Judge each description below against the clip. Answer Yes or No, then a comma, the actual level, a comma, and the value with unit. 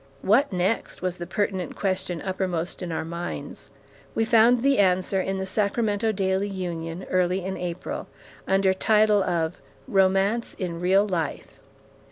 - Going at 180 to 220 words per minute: No, average, 145 wpm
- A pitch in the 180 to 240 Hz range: Yes, high, 190 Hz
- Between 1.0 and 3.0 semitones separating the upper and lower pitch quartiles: Yes, narrow, 2.4 semitones